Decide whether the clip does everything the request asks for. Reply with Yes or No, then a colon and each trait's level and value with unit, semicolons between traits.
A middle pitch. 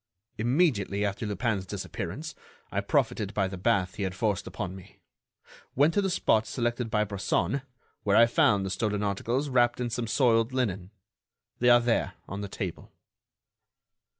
No: low, 110 Hz